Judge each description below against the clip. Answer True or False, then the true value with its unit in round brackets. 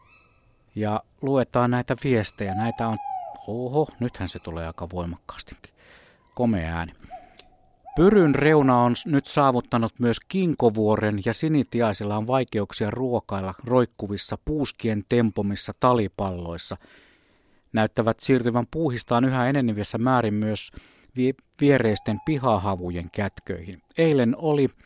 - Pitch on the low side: True (115 Hz)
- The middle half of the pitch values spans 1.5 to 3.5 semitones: False (4.1 semitones)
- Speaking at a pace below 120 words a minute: True (105 wpm)